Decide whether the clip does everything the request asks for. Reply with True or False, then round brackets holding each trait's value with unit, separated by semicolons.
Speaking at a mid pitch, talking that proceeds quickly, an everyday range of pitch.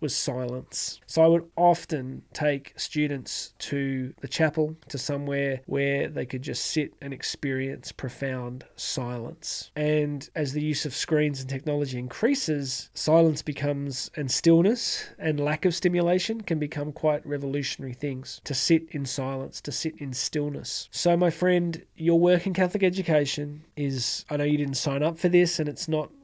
False (150 Hz; 165 wpm; 3.0 semitones)